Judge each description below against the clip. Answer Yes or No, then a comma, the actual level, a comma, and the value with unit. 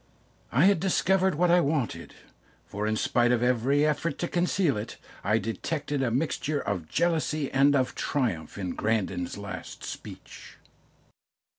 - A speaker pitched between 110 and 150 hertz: Yes, low, 135 Hz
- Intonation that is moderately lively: No, wide, 6.4 semitones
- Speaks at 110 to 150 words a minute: Yes, average, 145 wpm